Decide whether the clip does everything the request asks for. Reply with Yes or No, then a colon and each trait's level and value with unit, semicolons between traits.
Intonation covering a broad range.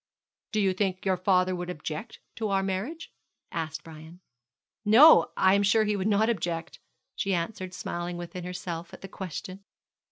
No: narrow, 2.6 semitones